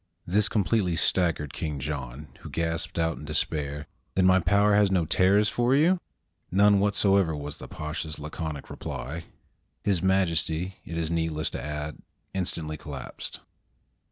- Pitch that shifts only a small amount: No, average, 4.1 semitones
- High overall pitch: No, very low, 85 Hz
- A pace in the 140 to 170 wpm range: Yes, average, 145 wpm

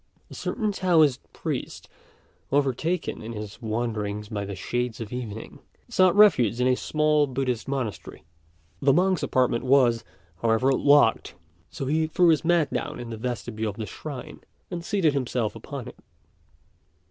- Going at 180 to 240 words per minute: No, average, 150 wpm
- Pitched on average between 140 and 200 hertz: No, low, 130 Hz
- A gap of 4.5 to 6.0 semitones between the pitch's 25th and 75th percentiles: Yes, average, 5.2 semitones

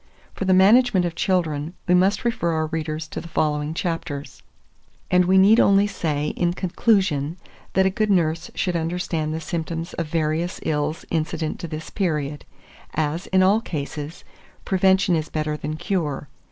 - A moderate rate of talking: Yes, average, 165 wpm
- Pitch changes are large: No, average, 3.4 semitones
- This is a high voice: No, medium, 170 Hz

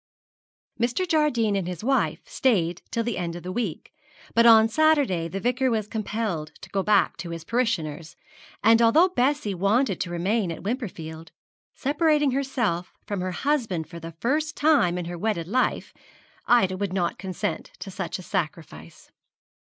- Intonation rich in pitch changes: Yes, wide, 6.2 semitones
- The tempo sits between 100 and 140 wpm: No, average, 165 wpm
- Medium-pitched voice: No, high, 210 Hz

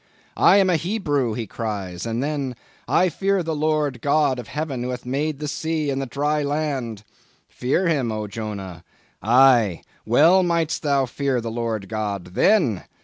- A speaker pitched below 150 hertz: Yes, low, 135 Hz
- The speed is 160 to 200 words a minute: Yes, average, 165 wpm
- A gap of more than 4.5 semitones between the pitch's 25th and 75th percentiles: Yes, average, 5.3 semitones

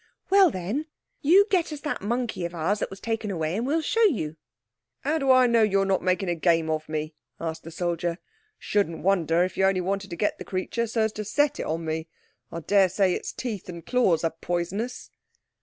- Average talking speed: No, fast, 210 wpm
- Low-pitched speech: No, high, 195 Hz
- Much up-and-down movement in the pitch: Yes, wide, 5.9 semitones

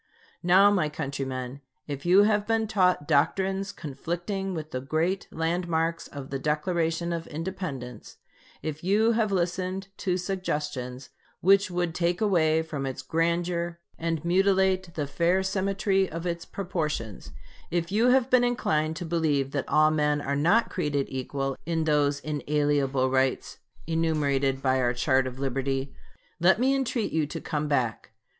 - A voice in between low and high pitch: Yes, medium, 165 Hz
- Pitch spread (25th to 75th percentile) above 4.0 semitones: Yes, average, 4.8 semitones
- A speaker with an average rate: Yes, average, 150 wpm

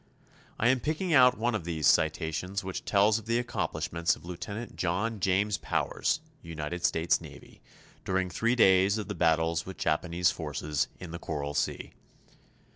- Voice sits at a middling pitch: No, very low, 90 Hz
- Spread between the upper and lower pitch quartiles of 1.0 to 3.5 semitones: No, average, 4.7 semitones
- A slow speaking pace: No, average, 160 wpm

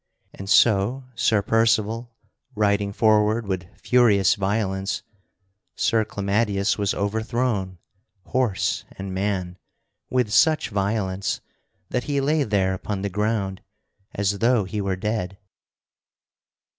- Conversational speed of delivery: No, slow, 110 wpm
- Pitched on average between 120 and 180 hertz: No, low, 105 Hz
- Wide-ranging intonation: No, average, 2.7 semitones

